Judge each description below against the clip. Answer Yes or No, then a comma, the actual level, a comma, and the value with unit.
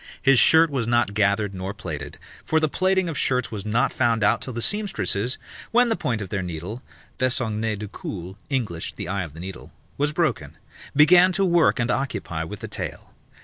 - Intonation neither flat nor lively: No, wide, 7.1 semitones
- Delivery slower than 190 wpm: No, average, 195 wpm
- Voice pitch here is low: Yes, low, 115 Hz